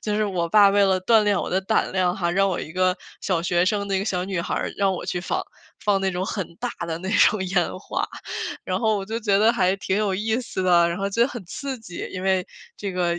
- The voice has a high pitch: Yes, high, 195 Hz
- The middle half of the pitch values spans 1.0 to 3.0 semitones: Yes, narrow, 2.5 semitones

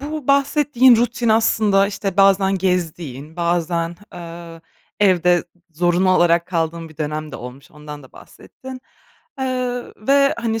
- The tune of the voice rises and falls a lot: Yes, wide, 6.0 semitones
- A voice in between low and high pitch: Yes, medium, 180 Hz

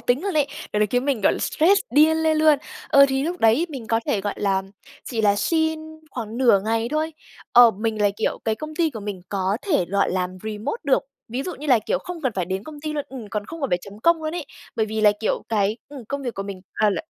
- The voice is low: No, high, 235 Hz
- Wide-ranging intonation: Yes, wide, 6.6 semitones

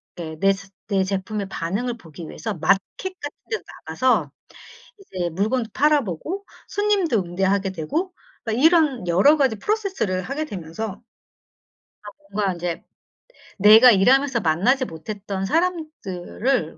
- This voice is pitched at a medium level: No, high, 210 Hz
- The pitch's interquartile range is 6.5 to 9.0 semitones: Yes, wide, 6.8 semitones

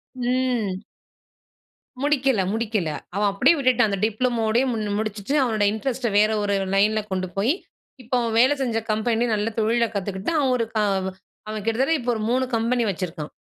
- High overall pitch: Yes, high, 225 Hz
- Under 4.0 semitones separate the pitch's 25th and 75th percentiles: Yes, average, 3.4 semitones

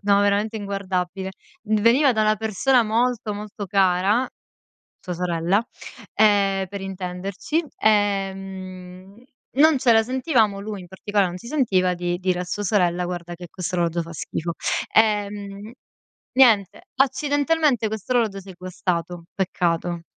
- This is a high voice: Yes, high, 200 Hz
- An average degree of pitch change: Yes, average, 3.3 semitones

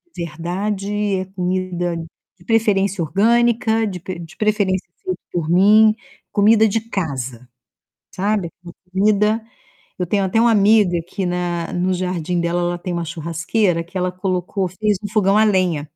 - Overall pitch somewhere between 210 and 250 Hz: No, medium, 185 Hz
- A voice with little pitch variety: No, average, 3.1 semitones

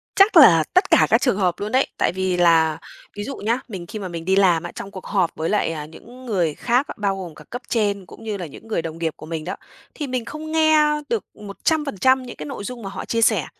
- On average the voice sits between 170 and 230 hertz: Yes, high, 200 Hz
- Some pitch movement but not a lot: No, wide, 6.5 semitones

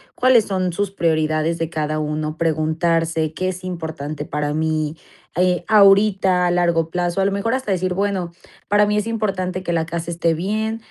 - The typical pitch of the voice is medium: Yes, medium, 175 Hz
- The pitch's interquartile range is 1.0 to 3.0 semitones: No, average, 3.6 semitones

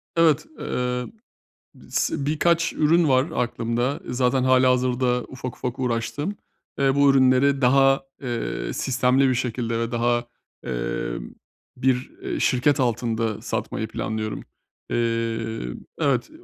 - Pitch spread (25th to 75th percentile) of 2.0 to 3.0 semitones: Yes, narrow, 2.5 semitones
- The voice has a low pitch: Yes, low, 125 Hz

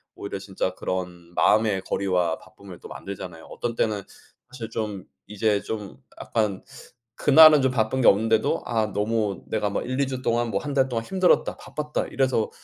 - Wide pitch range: No, average, 4.2 semitones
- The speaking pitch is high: No, low, 110 Hz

